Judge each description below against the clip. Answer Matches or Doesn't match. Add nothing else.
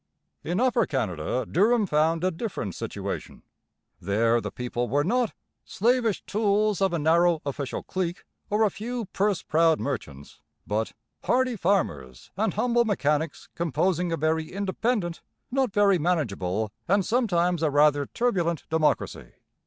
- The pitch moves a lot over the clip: Matches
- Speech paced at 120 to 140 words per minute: Matches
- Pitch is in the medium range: Matches